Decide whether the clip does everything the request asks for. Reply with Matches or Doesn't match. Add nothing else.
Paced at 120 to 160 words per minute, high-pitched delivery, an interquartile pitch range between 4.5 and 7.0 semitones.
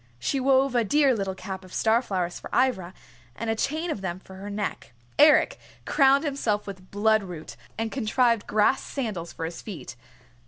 Doesn't match